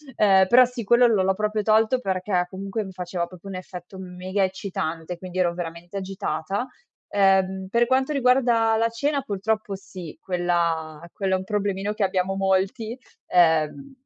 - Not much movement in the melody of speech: No, average, 3.2 semitones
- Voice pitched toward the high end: Yes, high, 195 Hz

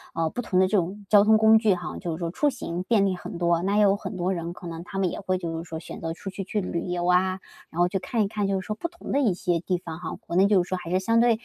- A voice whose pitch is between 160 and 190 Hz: Yes, medium, 185 Hz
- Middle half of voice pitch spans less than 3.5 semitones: Yes, average, 3.0 semitones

